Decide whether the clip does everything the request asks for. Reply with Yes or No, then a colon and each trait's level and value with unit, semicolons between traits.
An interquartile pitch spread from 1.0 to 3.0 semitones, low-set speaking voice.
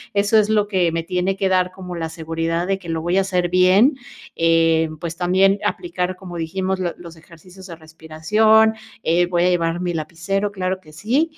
No: narrow, 2.6 semitones; medium, 180 Hz